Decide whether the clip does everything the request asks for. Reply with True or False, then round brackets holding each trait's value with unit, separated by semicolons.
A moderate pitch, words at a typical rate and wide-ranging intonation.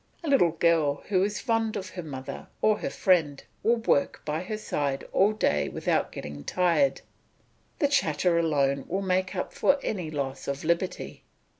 True (175 Hz; 170 wpm; 6.0 semitones)